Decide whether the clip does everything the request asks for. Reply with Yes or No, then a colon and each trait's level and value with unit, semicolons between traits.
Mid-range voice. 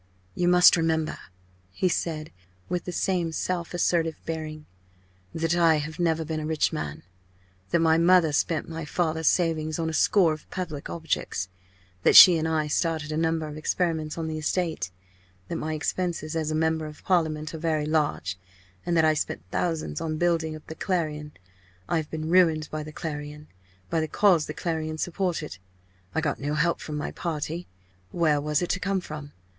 Yes: medium, 160 Hz